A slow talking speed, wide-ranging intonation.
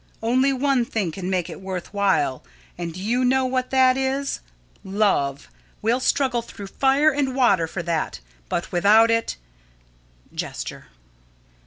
No: average, 145 wpm; wide, 5.9 semitones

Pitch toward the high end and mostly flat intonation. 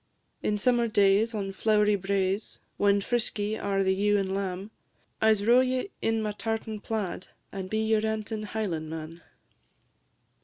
Yes: high, 210 Hz; narrow, 2.1 semitones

